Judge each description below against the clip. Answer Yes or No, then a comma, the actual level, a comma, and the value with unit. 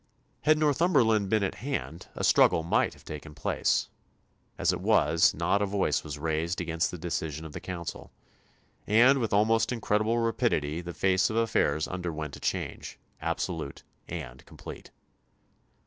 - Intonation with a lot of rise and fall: Yes, wide, 6.0 semitones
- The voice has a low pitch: Yes, very low, 90 Hz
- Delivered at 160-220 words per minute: No, average, 150 wpm